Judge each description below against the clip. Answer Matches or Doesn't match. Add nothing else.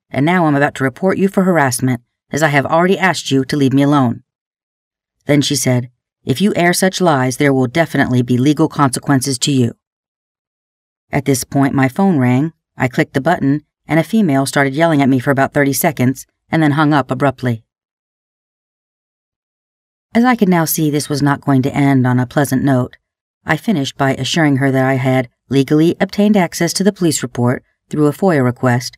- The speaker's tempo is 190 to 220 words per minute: Matches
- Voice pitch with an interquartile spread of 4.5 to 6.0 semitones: Doesn't match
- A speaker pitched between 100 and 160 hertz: Matches